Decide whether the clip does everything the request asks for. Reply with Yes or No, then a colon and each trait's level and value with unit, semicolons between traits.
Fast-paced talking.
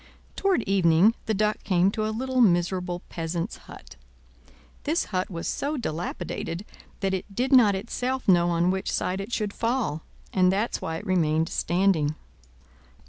No: average, 155 wpm